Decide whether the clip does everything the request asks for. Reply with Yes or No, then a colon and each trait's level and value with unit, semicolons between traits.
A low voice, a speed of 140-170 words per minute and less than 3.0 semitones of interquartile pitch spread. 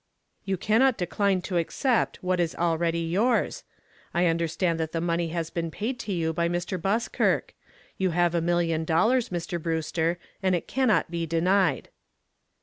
No: medium, 175 Hz; average, 160 wpm; narrow, 2.5 semitones